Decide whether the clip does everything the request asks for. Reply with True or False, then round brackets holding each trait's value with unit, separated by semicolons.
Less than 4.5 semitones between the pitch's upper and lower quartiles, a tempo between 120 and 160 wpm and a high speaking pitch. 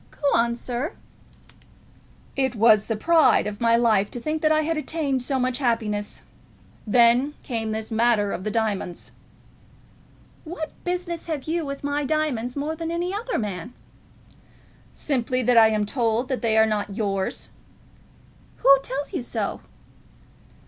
False (5.4 semitones; 155 wpm; 245 Hz)